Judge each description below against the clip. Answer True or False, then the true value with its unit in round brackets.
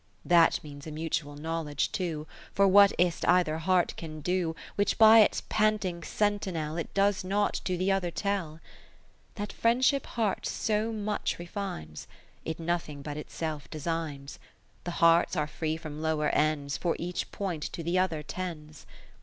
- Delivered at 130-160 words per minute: False (170 wpm)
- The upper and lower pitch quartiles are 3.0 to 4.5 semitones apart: True (4.1 semitones)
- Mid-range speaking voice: True (170 Hz)